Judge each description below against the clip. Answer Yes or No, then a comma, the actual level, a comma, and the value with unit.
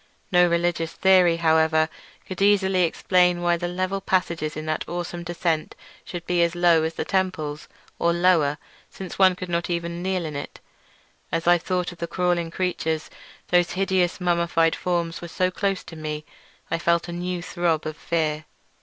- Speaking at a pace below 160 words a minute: No, average, 170 wpm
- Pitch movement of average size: No, narrow, 1.6 semitones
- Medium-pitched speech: Yes, medium, 175 Hz